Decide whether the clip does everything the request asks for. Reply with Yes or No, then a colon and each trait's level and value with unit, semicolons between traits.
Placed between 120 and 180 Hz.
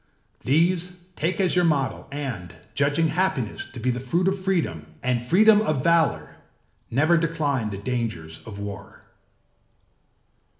Yes: medium, 140 Hz